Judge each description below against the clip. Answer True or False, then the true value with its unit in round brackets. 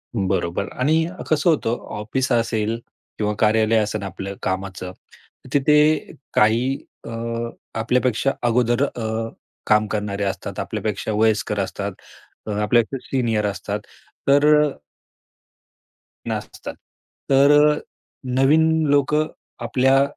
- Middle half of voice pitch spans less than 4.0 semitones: False (4.3 semitones)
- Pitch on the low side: True (115 Hz)